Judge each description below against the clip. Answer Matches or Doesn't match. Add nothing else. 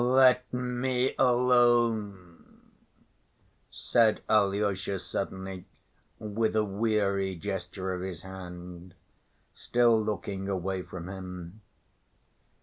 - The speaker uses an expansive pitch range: Doesn't match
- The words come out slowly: Matches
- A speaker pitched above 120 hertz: Doesn't match